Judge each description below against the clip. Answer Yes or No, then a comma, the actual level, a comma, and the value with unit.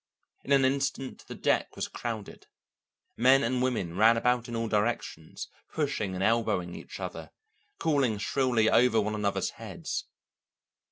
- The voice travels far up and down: No, average, 3.4 semitones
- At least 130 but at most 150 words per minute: Yes, average, 145 wpm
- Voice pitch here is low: Yes, low, 115 Hz